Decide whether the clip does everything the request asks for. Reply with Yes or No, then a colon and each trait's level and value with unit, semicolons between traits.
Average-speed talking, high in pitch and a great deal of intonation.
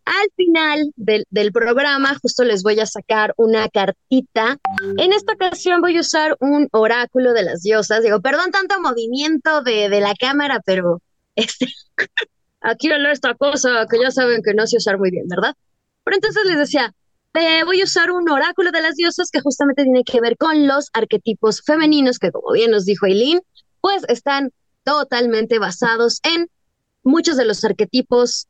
Yes: average, 180 wpm; very high, 255 Hz; wide, 5.9 semitones